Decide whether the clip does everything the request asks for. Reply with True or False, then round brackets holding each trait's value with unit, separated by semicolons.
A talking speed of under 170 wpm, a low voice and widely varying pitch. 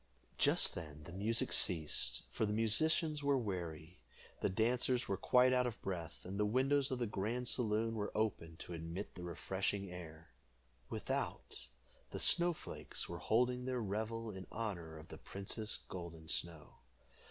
True (160 wpm; 105 Hz; 5.8 semitones)